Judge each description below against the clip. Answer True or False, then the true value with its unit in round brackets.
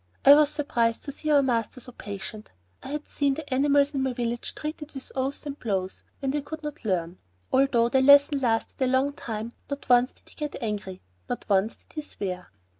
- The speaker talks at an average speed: False (210 wpm)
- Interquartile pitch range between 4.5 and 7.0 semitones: False (4.0 semitones)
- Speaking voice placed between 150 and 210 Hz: False (265 Hz)